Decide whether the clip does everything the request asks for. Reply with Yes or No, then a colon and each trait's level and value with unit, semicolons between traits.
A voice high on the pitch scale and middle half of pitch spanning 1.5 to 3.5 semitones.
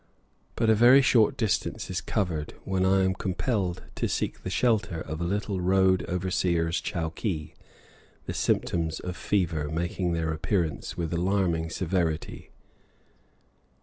No: very low, 90 Hz; average, 3.0 semitones